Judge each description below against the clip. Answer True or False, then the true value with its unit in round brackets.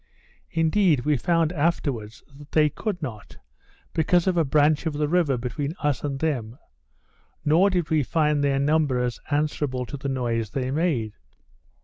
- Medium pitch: True (150 Hz)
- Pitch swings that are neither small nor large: True (3.6 semitones)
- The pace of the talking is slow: False (155 wpm)